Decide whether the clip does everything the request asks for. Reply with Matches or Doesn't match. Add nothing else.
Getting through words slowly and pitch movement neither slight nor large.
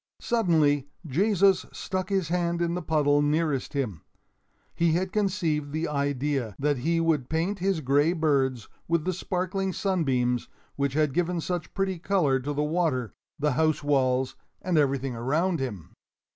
Doesn't match